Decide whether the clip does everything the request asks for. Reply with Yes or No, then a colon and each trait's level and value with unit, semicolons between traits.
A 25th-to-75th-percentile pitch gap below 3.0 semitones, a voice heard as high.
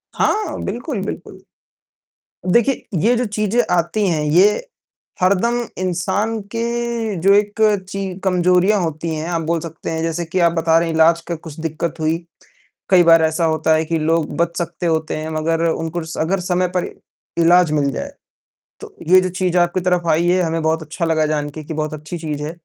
No: narrow, 2.6 semitones; medium, 170 Hz